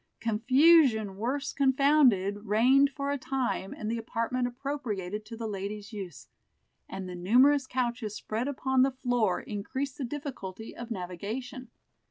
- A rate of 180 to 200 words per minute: No, average, 140 wpm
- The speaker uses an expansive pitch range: No, average, 4.3 semitones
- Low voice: No, high, 240 Hz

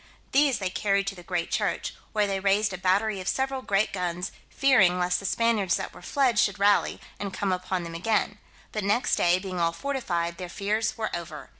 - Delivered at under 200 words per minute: No, fast, 205 wpm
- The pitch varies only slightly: No, average, 3.2 semitones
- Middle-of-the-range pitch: No, high, 195 Hz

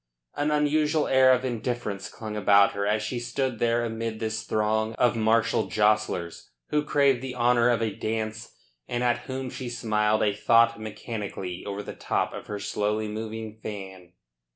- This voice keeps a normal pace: Yes, average, 170 wpm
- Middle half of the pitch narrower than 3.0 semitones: Yes, narrow, 2.4 semitones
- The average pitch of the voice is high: No, low, 110 Hz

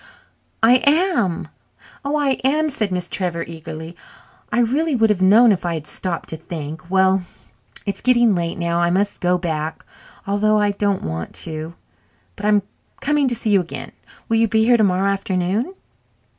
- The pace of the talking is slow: No, average, 170 wpm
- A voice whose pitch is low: No, high, 195 Hz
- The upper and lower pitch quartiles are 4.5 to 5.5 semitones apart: Yes, average, 5.0 semitones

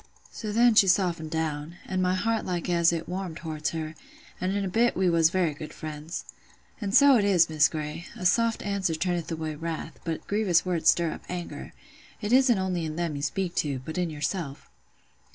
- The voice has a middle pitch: Yes, medium, 175 Hz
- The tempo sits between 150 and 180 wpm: No, fast, 205 wpm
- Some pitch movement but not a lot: Yes, average, 3.3 semitones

